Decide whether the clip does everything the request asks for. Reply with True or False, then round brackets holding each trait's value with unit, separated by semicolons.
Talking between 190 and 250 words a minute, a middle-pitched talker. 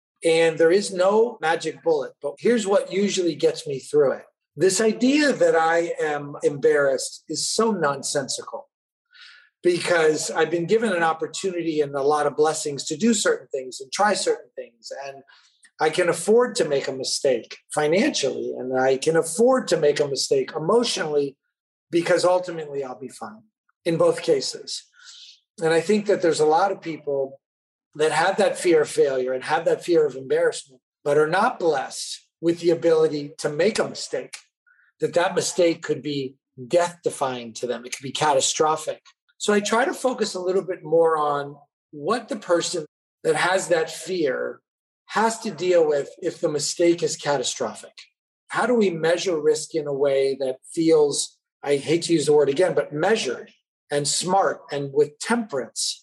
False (175 wpm; 175 Hz)